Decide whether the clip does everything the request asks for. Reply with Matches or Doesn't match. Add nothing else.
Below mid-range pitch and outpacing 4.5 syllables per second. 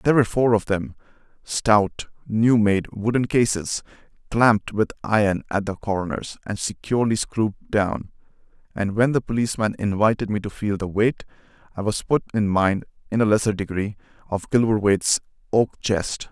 Matches